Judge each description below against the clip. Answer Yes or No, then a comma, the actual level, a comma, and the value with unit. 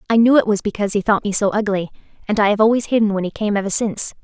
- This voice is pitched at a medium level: No, high, 210 Hz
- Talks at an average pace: No, fast, 285 wpm